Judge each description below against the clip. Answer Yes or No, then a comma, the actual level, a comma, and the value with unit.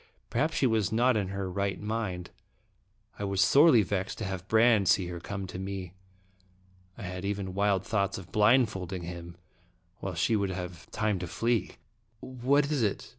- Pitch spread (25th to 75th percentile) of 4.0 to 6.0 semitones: No, average, 3.3 semitones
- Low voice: Yes, low, 100 Hz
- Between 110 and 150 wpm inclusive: No, average, 175 wpm